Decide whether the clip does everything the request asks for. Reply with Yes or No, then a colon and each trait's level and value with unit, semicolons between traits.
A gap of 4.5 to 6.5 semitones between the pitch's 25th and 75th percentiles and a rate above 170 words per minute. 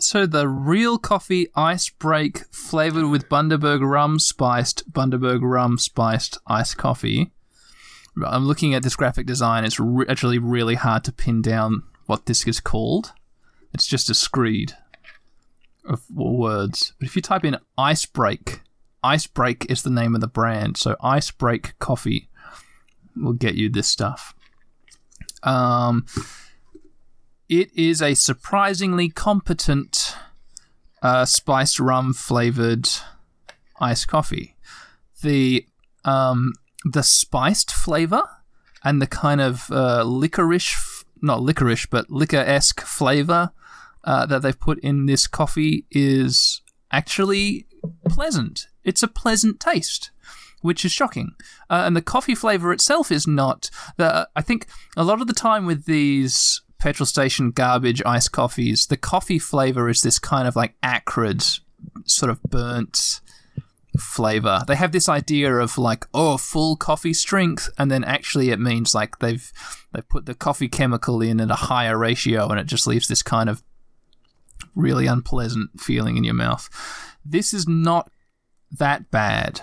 No: average, 5.1 semitones; average, 145 wpm